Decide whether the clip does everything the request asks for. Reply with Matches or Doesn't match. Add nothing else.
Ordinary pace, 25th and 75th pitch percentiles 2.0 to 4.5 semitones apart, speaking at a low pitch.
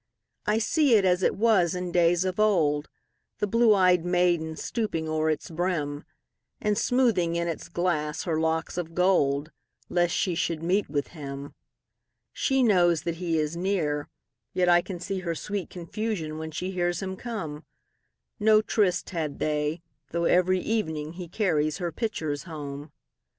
Doesn't match